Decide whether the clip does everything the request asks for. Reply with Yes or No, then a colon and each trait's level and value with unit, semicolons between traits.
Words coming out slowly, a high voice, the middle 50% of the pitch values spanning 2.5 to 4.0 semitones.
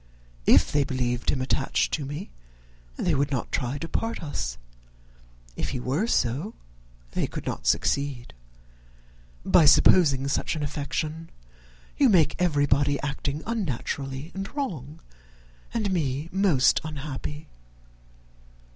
No: slow, 120 wpm; medium, 145 Hz; average, 3.7 semitones